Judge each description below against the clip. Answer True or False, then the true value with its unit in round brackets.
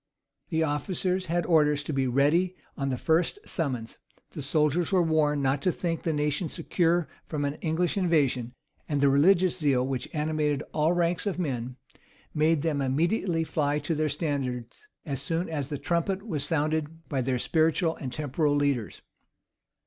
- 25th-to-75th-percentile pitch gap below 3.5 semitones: True (2.9 semitones)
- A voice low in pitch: False (155 Hz)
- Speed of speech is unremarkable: True (165 wpm)